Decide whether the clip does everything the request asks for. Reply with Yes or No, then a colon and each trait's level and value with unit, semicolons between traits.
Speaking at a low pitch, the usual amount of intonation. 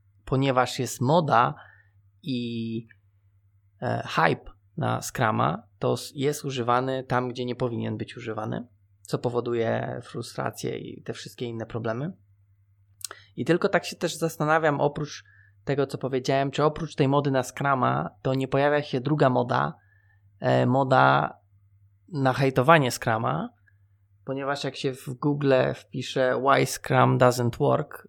No: low, 125 Hz; wide, 5.7 semitones